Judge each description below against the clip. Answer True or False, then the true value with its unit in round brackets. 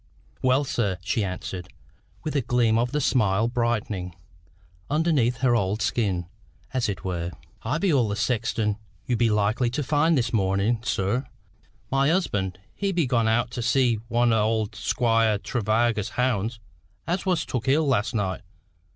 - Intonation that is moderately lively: True (3.8 semitones)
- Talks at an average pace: True (160 wpm)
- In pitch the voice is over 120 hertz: False (115 Hz)